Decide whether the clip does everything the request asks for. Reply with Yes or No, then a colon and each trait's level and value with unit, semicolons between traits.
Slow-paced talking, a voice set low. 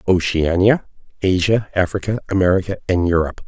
Yes: slow, 105 wpm; very low, 95 Hz